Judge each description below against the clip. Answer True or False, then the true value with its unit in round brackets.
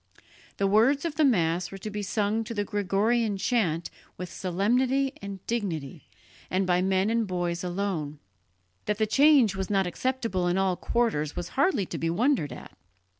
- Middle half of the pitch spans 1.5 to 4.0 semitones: False (4.5 semitones)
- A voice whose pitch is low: False (200 Hz)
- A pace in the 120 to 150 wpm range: False (175 wpm)